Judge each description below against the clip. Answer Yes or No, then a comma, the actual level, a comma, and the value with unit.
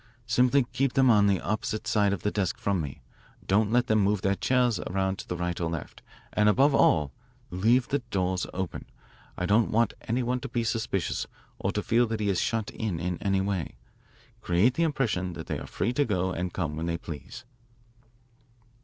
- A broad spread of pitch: No, average, 4.7 semitones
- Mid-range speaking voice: No, low, 100 Hz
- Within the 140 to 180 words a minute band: No, fast, 205 wpm